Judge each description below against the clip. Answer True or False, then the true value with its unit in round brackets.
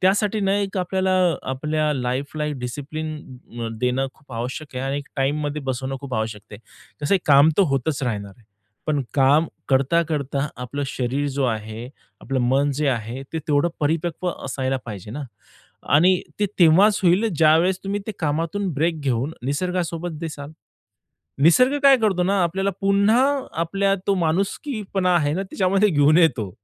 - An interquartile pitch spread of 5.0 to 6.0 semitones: True (5.4 semitones)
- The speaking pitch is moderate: True (150 Hz)